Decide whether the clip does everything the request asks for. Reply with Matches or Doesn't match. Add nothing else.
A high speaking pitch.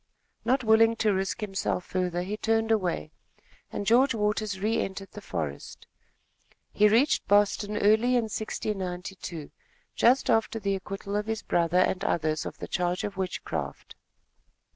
Matches